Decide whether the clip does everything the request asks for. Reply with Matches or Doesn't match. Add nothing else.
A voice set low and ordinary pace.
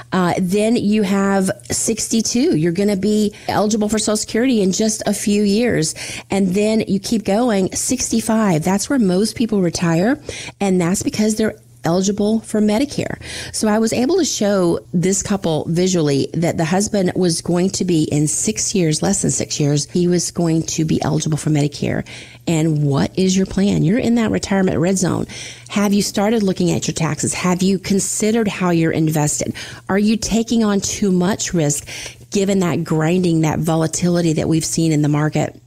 Doesn't match